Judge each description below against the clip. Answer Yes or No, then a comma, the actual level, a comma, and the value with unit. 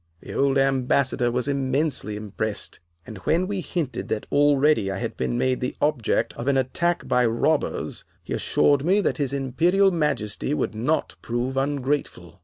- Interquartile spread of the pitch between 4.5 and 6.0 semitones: No, average, 3.9 semitones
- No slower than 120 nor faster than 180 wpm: Yes, average, 165 wpm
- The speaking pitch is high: No, low, 135 Hz